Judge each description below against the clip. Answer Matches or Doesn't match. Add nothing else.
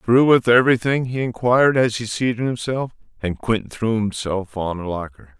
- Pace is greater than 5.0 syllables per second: Matches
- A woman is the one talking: Doesn't match